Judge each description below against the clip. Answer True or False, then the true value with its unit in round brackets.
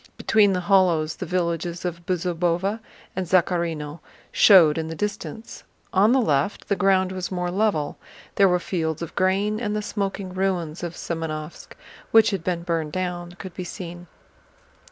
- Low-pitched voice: False (180 Hz)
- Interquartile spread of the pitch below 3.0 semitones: True (2.5 semitones)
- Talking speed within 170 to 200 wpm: False (160 wpm)